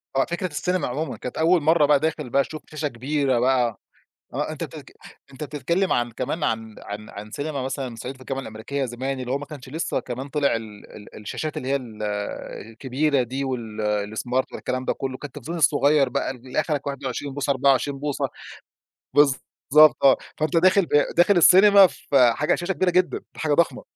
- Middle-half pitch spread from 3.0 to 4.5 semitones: Yes, average, 3.4 semitones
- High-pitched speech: No, medium, 140 Hz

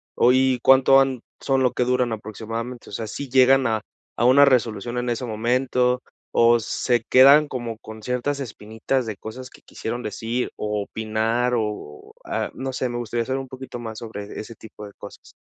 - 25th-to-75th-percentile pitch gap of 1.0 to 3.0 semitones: Yes, narrow, 2.6 semitones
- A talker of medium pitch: No, low, 120 Hz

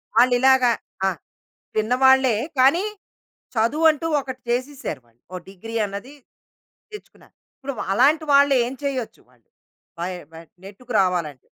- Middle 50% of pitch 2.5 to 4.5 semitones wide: No, wide, 5.5 semitones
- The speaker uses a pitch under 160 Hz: No, very high, 255 Hz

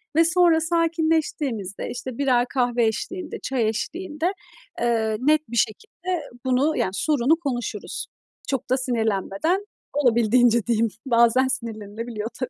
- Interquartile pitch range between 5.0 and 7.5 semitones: Yes, wide, 5.6 semitones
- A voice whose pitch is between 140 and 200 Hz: No, very high, 250 Hz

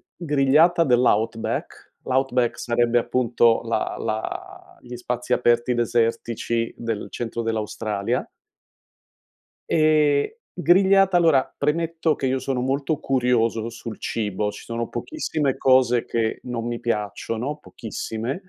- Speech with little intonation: No, average, 3.5 semitones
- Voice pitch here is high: No, low, 125 Hz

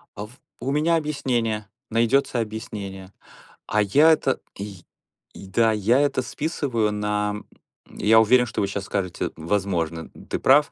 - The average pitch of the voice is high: No, low, 110 Hz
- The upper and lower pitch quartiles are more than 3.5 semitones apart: Yes, average, 4.3 semitones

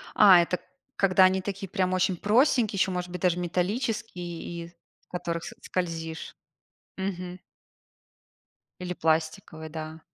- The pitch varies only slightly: Yes, narrow, 2.3 semitones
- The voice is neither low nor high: Yes, medium, 180 Hz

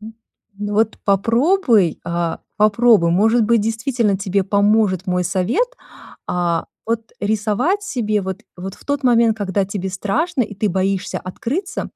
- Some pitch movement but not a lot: Yes, average, 3.5 semitones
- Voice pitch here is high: Yes, high, 210 Hz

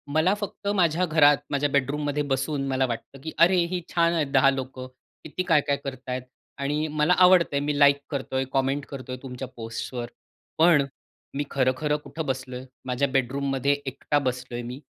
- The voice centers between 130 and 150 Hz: Yes, medium, 140 Hz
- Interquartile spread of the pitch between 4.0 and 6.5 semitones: No, narrow, 2.4 semitones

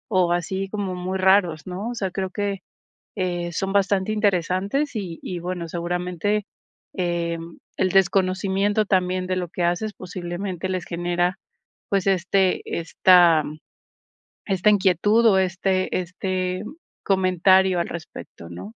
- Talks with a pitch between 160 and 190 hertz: Yes, medium, 185 Hz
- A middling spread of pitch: No, narrow, 1.8 semitones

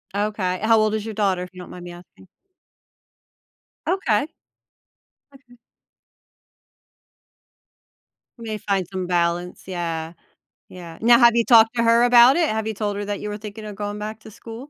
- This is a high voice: Yes, high, 210 Hz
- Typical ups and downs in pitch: Yes, average, 3.9 semitones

